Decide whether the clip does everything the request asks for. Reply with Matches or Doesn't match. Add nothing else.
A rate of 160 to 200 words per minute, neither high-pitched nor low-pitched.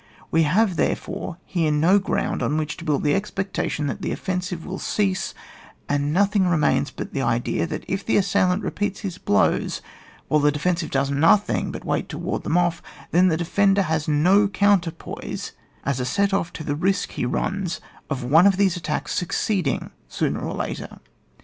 Matches